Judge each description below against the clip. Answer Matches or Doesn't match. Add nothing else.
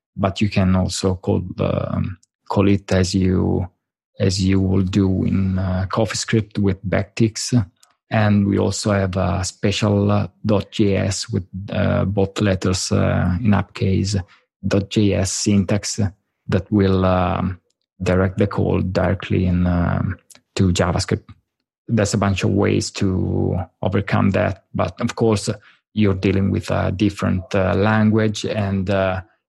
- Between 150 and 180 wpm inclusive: Doesn't match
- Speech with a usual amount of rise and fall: Doesn't match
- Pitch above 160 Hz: Doesn't match